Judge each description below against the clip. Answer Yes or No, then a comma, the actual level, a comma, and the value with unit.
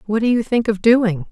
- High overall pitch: Yes, high, 220 Hz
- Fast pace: Yes, fast, 275 wpm